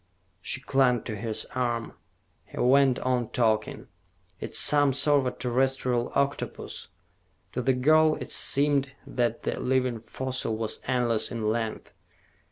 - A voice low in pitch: Yes, low, 125 Hz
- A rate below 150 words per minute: Yes, average, 140 wpm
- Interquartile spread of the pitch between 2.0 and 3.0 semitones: Yes, narrow, 2.5 semitones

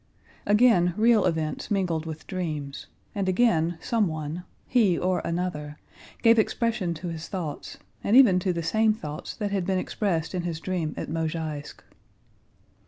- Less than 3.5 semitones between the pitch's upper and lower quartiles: No, average, 4.2 semitones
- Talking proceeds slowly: No, average, 150 wpm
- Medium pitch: Yes, medium, 175 Hz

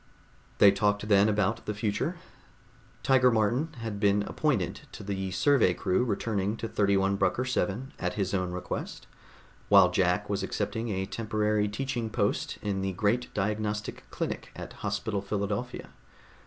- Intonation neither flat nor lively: No, narrow, 2.3 semitones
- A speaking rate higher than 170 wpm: No, average, 145 wpm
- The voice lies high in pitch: No, low, 105 Hz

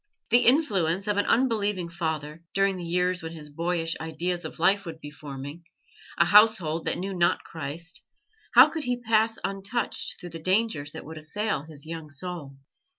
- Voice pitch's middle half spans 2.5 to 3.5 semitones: No, average, 4.1 semitones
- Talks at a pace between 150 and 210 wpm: Yes, average, 175 wpm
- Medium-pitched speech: Yes, medium, 175 Hz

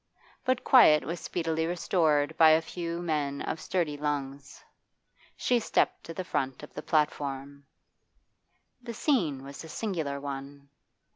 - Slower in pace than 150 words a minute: Yes, average, 140 wpm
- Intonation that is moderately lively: Yes, average, 3.4 semitones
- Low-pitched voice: No, medium, 155 Hz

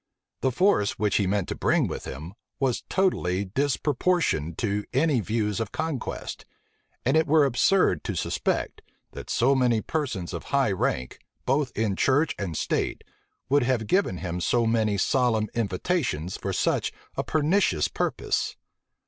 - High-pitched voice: No, low, 120 Hz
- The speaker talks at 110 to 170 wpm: Yes, average, 150 wpm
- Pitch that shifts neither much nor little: No, wide, 6.3 semitones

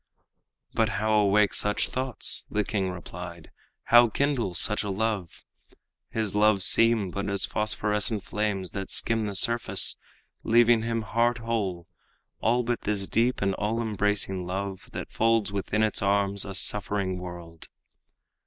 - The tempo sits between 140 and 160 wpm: Yes, average, 145 wpm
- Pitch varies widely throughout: No, narrow, 2.6 semitones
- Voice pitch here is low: Yes, low, 105 Hz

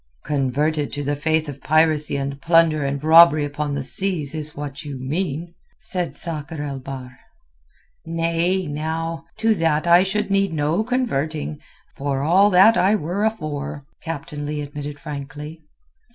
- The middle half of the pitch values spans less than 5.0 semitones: Yes, average, 2.7 semitones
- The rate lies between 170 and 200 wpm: No, average, 150 wpm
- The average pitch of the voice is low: No, medium, 155 Hz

